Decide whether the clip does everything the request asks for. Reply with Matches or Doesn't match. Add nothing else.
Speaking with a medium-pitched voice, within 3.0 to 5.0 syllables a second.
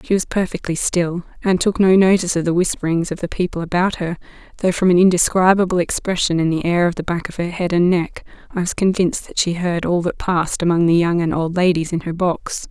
Doesn't match